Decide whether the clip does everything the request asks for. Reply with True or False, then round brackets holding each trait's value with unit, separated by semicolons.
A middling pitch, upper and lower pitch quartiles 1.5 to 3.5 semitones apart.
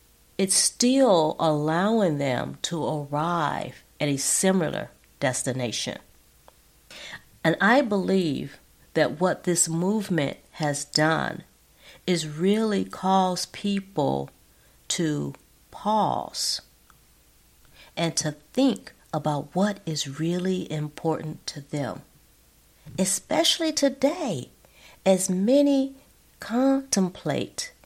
False (175 Hz; 5.2 semitones)